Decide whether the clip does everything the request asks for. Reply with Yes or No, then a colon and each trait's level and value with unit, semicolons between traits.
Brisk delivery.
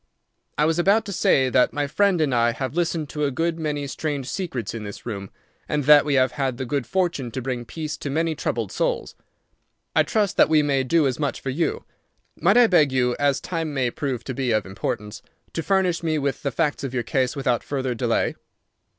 Yes: fast, 220 wpm